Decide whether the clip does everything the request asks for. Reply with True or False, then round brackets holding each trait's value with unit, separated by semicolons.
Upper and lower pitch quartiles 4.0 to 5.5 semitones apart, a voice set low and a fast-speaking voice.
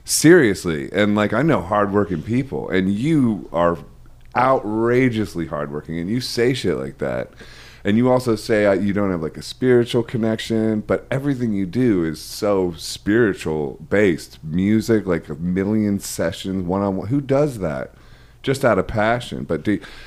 False (4.6 semitones; 105 Hz; 160 wpm)